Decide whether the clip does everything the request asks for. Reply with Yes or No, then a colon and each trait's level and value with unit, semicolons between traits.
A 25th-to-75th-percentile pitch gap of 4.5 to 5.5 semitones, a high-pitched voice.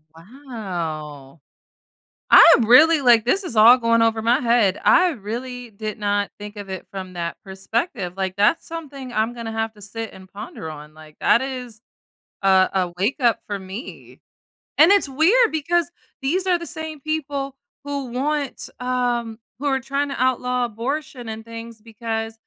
Yes: average, 5.2 semitones; high, 235 Hz